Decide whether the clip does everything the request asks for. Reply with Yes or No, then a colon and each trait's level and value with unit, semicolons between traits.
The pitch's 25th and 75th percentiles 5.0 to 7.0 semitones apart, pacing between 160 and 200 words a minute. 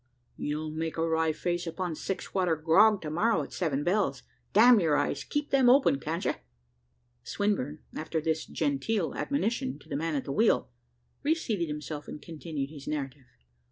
Yes: average, 5.3 semitones; average, 170 wpm